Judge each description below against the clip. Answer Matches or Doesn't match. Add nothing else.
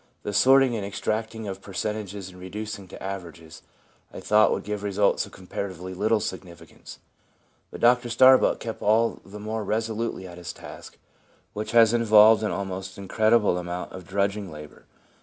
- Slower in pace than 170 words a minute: Matches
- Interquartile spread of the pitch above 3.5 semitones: Doesn't match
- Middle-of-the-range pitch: Doesn't match